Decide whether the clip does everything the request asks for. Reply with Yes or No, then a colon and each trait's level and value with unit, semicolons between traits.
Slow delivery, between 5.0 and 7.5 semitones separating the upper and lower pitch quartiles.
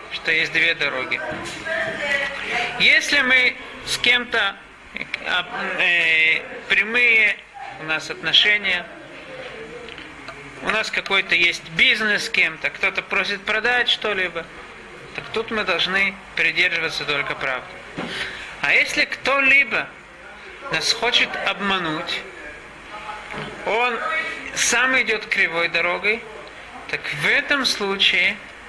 Yes: slow, 100 wpm; average, 5.3 semitones